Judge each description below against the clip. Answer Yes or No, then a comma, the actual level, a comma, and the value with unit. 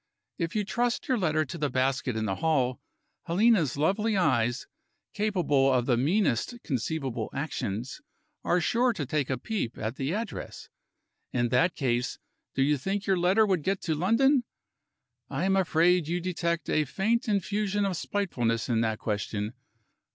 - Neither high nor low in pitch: Yes, medium, 160 Hz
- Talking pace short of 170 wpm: Yes, average, 160 wpm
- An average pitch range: No, wide, 7.4 semitones